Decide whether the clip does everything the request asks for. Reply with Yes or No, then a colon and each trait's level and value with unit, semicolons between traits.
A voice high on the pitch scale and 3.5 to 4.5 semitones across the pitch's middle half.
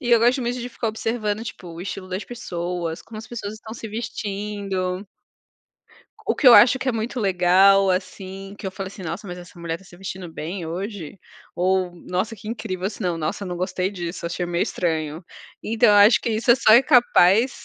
Yes: high, 195 Hz; average, 3.8 semitones